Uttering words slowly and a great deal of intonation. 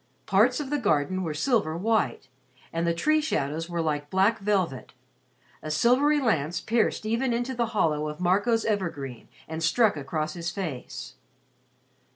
No: average, 155 wpm; wide, 6.8 semitones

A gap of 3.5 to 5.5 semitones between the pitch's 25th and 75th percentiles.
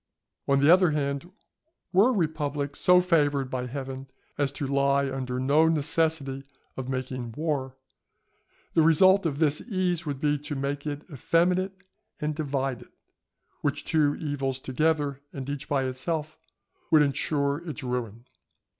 No: average, 2.9 semitones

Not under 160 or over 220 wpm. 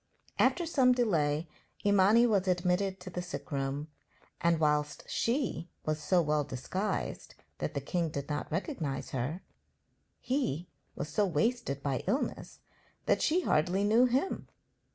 No: average, 140 wpm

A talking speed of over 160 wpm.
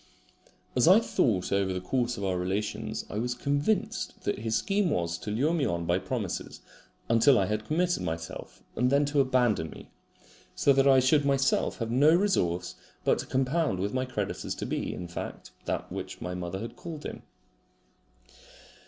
Yes: average, 180 wpm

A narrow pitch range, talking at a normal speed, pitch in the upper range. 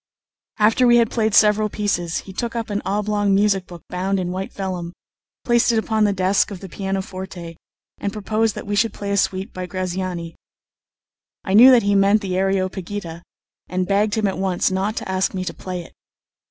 Yes: narrow, 2.2 semitones; average, 195 wpm; high, 195 Hz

